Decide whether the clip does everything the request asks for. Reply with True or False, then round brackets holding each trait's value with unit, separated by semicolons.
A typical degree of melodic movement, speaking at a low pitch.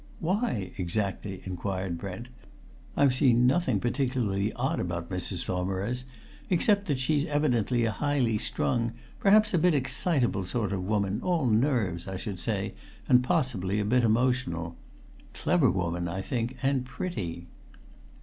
False (5.8 semitones; 115 Hz)